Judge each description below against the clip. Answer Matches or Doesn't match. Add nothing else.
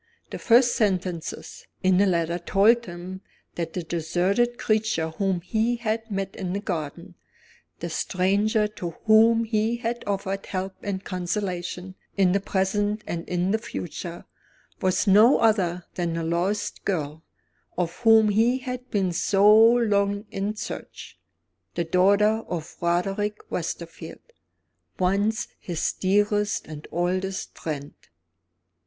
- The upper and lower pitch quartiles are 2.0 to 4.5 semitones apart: Matches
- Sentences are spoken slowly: Matches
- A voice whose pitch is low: Doesn't match